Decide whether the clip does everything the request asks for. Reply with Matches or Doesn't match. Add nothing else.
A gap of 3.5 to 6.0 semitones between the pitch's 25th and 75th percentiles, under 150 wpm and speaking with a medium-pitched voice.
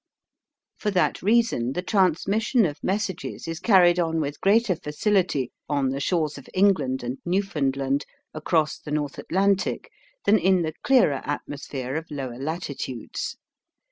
Matches